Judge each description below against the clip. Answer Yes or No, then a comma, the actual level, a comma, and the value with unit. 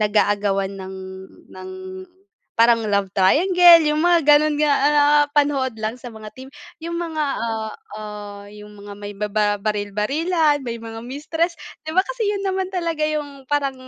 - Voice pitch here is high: Yes, very high, 260 Hz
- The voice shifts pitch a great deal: Yes, wide, 7.0 semitones